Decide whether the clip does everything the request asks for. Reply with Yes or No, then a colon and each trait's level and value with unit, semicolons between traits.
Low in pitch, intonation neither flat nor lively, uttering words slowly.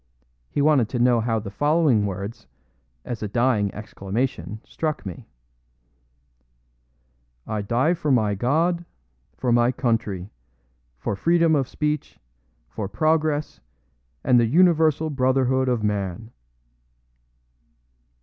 No: low, 125 Hz; wide, 6.1 semitones; slow, 110 wpm